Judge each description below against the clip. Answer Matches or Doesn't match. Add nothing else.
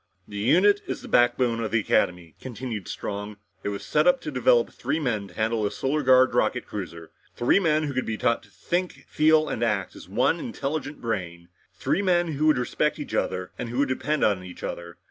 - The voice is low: Matches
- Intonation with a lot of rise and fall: Matches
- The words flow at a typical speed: Doesn't match